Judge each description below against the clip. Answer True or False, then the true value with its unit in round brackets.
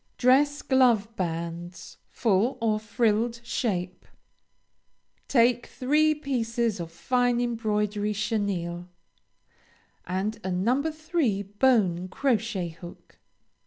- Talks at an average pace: False (90 wpm)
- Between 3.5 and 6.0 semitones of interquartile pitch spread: True (4.7 semitones)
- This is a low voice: False (220 Hz)